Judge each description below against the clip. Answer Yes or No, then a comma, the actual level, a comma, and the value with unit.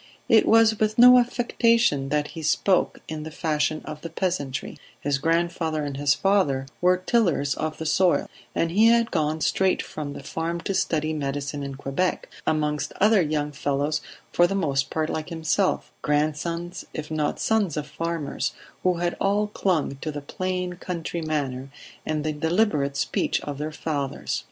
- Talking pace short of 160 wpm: No, average, 170 wpm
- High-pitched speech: No, medium, 160 Hz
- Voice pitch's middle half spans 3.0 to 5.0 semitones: Yes, average, 3.9 semitones